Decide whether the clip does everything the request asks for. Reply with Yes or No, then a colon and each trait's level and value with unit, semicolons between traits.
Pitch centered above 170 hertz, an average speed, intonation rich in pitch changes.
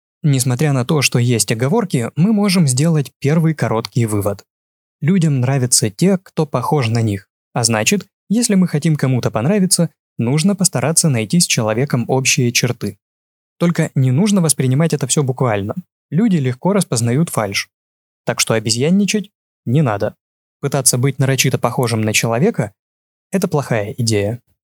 No: low, 135 Hz; average, 140 wpm; wide, 5.8 semitones